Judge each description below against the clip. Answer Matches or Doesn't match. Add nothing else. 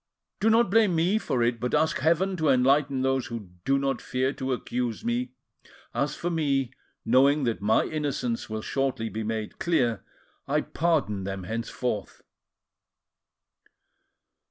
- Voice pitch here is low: Matches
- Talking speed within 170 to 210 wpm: Doesn't match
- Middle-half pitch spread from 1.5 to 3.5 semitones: Doesn't match